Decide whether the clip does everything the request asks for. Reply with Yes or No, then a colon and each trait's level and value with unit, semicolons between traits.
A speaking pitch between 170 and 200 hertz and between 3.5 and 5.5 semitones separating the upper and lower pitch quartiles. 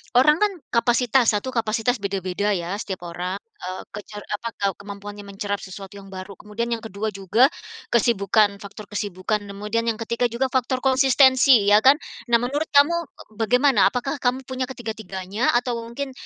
No: high, 225 Hz; average, 4.1 semitones